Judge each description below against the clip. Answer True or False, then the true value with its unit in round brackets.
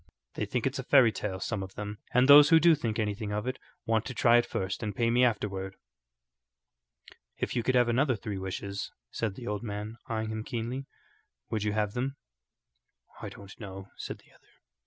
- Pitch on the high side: False (110 Hz)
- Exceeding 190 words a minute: True (200 wpm)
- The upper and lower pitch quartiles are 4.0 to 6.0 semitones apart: False (3.3 semitones)